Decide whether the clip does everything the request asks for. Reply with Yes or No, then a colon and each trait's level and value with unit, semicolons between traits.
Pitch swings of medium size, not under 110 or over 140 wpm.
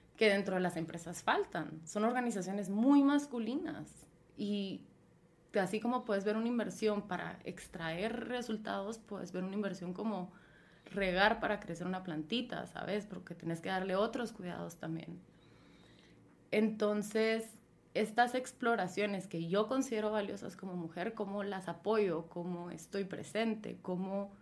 Yes: average, 3.7 semitones; average, 135 wpm